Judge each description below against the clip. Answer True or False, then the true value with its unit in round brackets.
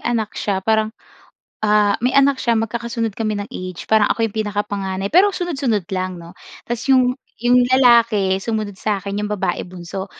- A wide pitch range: False (3.4 semitones)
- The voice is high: True (215 Hz)